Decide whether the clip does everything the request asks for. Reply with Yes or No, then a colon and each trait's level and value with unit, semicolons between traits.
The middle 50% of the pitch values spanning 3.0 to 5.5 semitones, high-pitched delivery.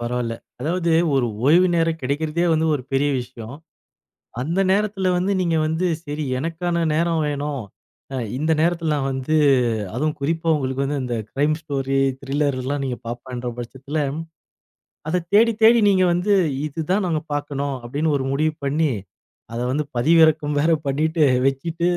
No: average, 3.5 semitones; medium, 150 Hz